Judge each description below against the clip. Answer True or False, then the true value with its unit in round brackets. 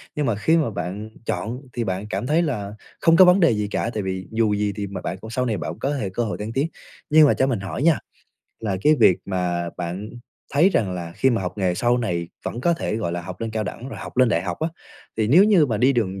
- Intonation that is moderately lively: False (5.9 semitones)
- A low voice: True (110 Hz)